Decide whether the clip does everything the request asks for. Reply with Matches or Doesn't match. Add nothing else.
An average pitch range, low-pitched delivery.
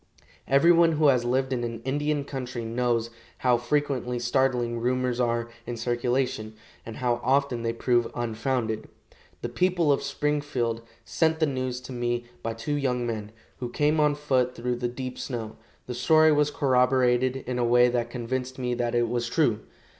Doesn't match